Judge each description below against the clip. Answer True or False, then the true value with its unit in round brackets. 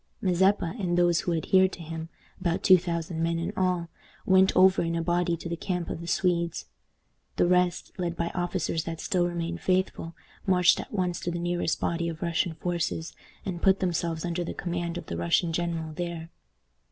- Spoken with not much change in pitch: True (1.3 semitones)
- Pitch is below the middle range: False (175 Hz)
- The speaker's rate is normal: True (195 wpm)